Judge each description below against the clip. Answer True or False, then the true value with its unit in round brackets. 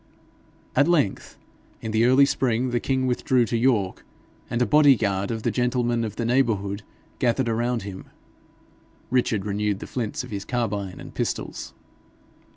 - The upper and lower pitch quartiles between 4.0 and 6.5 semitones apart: False (3.3 semitones)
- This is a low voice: True (120 Hz)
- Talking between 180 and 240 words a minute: False (160 wpm)